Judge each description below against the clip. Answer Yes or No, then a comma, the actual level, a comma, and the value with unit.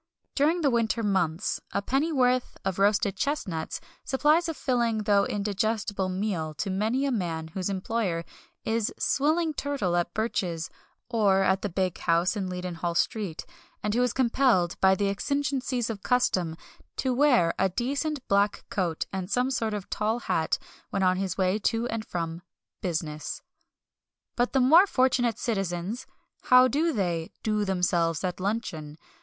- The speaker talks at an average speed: Yes, average, 155 wpm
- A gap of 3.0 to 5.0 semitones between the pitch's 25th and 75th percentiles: No, wide, 5.4 semitones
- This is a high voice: Yes, high, 205 Hz